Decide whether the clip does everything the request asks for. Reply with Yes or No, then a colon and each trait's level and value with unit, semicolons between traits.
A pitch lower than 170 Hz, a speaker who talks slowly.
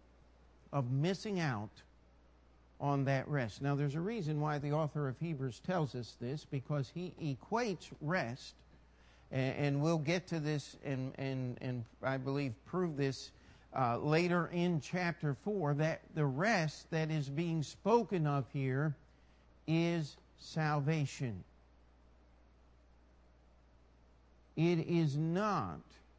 Yes: medium, 140 Hz; slow, 120 wpm